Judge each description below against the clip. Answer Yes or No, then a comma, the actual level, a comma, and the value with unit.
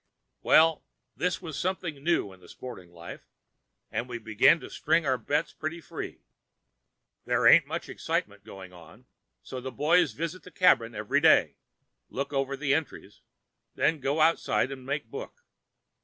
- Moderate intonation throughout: No, wide, 6.2 semitones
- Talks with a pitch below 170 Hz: Yes, medium, 140 Hz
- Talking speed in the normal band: Yes, average, 155 wpm